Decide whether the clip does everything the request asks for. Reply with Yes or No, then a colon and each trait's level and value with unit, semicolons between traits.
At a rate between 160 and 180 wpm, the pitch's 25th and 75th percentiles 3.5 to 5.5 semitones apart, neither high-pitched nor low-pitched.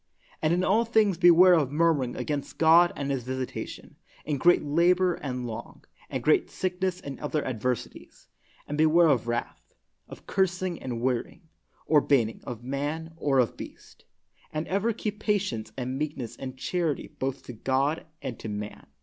Yes: average, 170 wpm; average, 5.2 semitones; medium, 150 Hz